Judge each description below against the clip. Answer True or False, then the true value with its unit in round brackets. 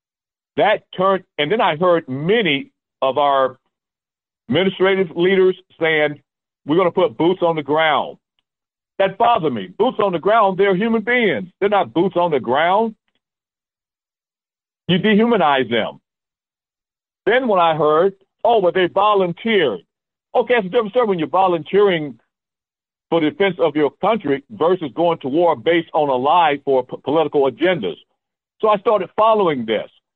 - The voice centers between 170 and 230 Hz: True (185 Hz)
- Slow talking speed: False (155 wpm)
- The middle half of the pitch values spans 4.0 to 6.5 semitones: True (4.4 semitones)